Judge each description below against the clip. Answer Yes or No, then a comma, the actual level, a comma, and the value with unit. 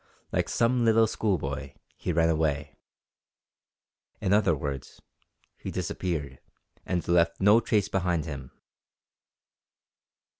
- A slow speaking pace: Yes, slow, 105 wpm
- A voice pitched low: Yes, very low, 85 Hz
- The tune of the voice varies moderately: No, wide, 6.1 semitones